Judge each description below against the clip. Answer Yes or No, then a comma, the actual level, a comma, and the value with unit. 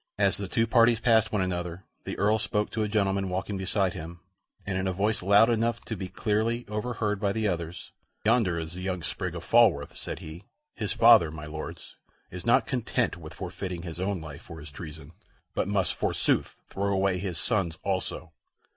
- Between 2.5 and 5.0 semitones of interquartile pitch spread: Yes, average, 3.5 semitones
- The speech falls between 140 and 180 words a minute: No, average, 195 wpm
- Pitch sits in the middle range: No, very low, 95 Hz